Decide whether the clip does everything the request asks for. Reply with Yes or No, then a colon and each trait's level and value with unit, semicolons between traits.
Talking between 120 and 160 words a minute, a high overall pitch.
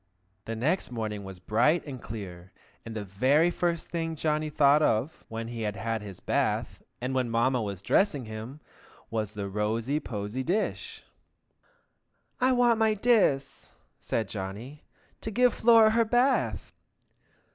No: average, 145 wpm; low, 130 Hz